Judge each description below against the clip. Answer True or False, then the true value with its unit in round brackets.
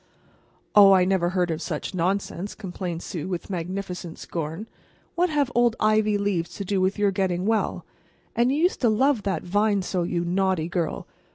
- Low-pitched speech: False (190 Hz)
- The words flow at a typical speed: True (180 wpm)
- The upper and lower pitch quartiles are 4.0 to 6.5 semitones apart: False (3.2 semitones)